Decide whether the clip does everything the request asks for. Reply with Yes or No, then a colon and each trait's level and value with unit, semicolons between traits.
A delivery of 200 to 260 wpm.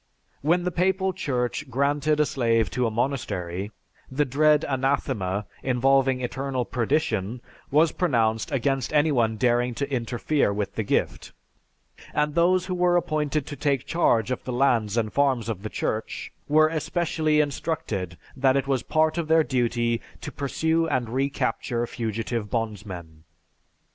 No: average, 145 wpm